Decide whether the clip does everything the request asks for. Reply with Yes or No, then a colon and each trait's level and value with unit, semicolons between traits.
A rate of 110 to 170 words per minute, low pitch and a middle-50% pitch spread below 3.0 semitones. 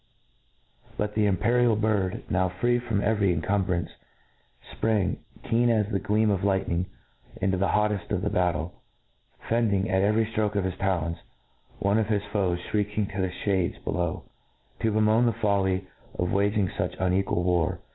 Yes: average, 165 wpm; low, 100 Hz; narrow, 2.5 semitones